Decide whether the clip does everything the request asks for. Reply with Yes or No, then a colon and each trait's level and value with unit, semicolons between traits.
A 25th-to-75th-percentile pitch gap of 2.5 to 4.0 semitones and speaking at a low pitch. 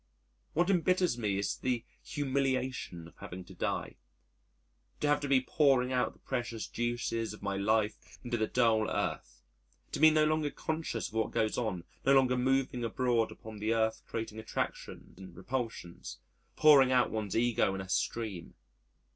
Yes: average, 3.5 semitones; low, 120 Hz